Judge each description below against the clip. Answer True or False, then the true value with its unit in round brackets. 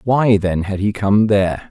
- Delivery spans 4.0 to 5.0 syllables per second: True (4.4 syllables/s)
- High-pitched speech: False (100 Hz)